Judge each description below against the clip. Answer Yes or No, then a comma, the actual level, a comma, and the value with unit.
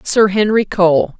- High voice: Yes, high, 195 Hz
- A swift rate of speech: No, average, 150 wpm